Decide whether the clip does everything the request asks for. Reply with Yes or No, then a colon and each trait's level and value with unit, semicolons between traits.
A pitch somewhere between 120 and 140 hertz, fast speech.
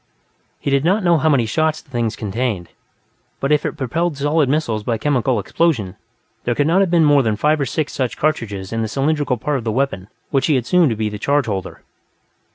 Yes: low, 135 Hz; fast, 225 wpm